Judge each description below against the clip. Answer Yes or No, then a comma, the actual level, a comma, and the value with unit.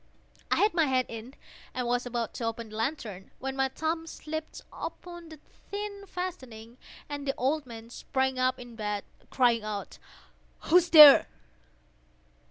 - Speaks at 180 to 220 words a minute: No, average, 150 wpm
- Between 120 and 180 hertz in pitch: No, very high, 260 Hz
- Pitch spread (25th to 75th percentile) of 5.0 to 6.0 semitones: Yes, average, 5.3 semitones